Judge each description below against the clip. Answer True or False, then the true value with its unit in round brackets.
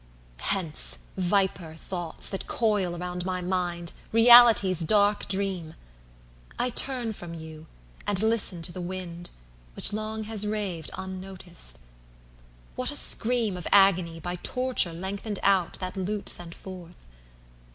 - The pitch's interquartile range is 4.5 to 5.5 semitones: False (3.3 semitones)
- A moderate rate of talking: False (110 wpm)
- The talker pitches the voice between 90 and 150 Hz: False (185 Hz)